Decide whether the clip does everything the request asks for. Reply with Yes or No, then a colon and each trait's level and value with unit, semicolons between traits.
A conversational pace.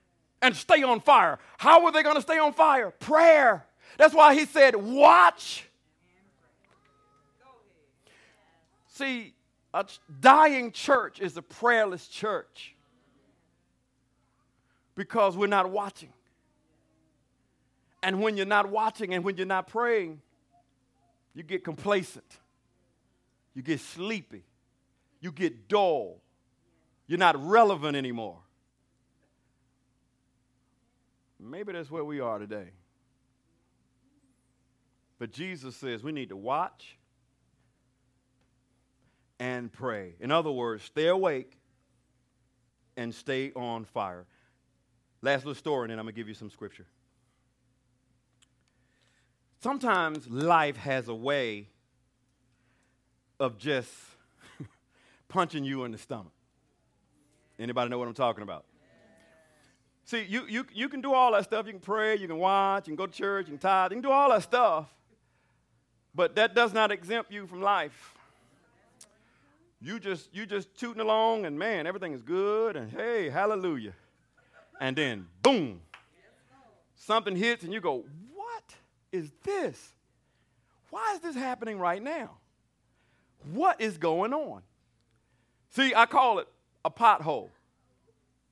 No: slow, 125 wpm